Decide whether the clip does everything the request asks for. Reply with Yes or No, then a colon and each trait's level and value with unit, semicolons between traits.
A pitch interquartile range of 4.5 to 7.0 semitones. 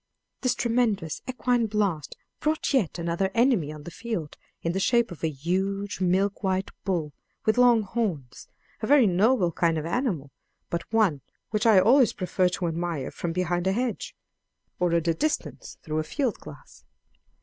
Yes: wide, 5.4 semitones